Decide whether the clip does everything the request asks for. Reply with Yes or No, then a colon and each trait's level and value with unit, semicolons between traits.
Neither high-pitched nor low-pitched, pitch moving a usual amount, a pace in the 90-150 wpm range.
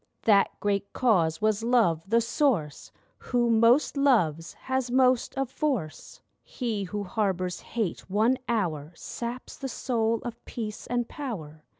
No: high, 225 Hz; average, 4.5 semitones; slow, 135 wpm